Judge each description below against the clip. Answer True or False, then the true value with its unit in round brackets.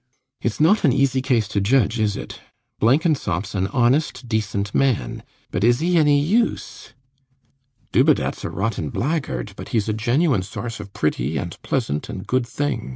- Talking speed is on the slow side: False (165 wpm)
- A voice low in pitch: True (120 Hz)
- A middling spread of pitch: False (5.7 semitones)